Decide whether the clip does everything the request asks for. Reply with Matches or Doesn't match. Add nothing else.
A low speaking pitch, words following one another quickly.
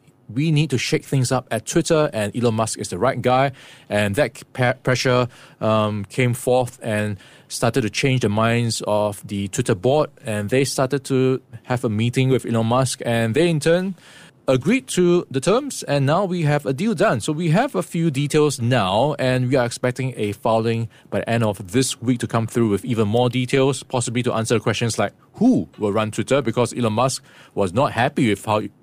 Matches